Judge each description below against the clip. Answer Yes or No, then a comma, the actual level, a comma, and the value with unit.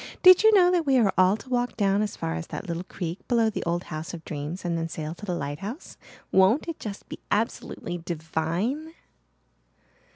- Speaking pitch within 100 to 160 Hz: No, high, 190 Hz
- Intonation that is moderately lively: No, wide, 6.6 semitones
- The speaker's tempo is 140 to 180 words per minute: No, average, 200 wpm